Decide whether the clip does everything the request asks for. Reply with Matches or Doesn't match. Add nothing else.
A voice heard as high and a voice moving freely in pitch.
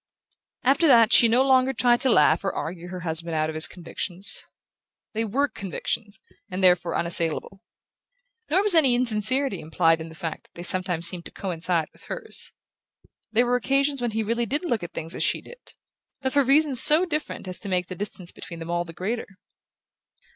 Matches